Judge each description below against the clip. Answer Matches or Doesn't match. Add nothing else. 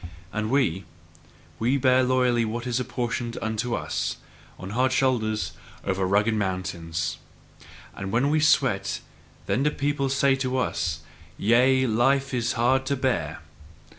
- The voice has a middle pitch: Doesn't match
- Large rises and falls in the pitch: Doesn't match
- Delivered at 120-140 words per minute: Matches